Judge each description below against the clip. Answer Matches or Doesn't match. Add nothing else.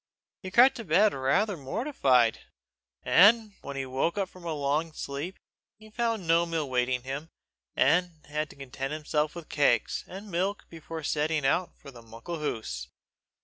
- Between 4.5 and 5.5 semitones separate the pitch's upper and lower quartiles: Matches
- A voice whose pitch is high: Doesn't match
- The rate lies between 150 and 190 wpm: Matches